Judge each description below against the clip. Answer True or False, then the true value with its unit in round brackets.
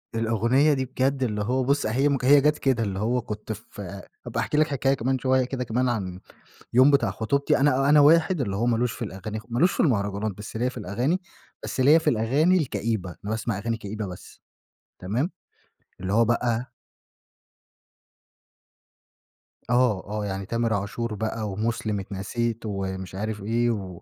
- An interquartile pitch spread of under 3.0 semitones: False (4.1 semitones)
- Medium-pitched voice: False (115 Hz)